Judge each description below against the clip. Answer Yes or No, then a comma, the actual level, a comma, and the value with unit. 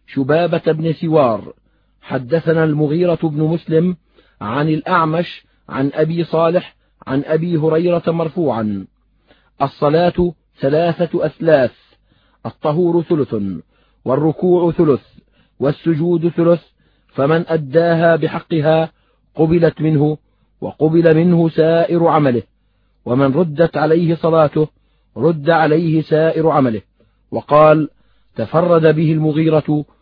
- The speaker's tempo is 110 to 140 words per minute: No, average, 90 wpm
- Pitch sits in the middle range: Yes, medium, 160 Hz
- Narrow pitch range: Yes, narrow, 1.8 semitones